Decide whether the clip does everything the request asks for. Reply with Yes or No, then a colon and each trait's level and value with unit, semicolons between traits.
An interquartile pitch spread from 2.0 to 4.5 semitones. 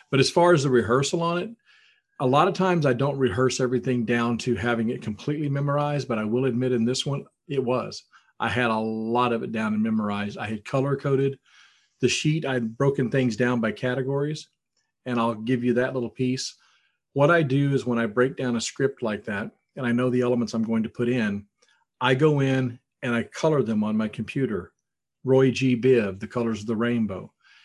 Yes: average, 2.8 semitones